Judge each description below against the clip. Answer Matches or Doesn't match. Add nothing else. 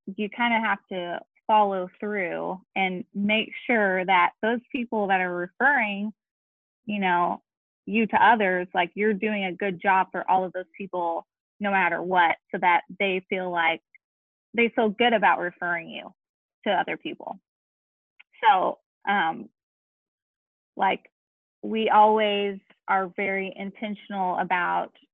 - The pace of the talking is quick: Doesn't match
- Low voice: Doesn't match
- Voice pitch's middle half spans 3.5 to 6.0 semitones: Doesn't match